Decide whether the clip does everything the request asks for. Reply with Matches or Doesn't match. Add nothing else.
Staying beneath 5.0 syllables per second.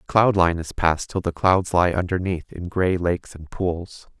Matches